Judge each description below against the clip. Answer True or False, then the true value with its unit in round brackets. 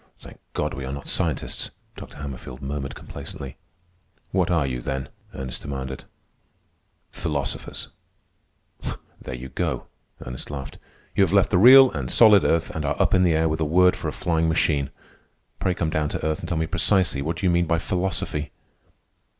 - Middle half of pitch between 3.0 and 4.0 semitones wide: False (4.4 semitones)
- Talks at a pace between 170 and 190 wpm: True (180 wpm)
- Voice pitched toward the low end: True (80 Hz)